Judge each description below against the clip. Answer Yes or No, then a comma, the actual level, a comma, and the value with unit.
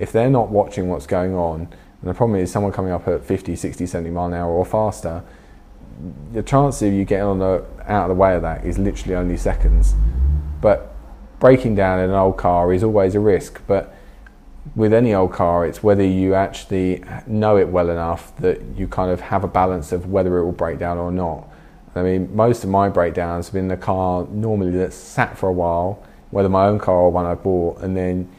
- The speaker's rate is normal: No, fast, 220 wpm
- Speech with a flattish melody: Yes, narrow, 2.2 semitones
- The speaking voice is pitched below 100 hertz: Yes, very low, 90 Hz